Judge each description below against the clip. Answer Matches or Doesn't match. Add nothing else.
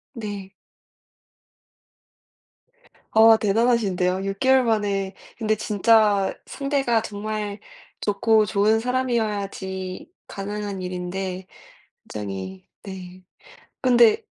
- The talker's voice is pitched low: Doesn't match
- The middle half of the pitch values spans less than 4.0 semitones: Matches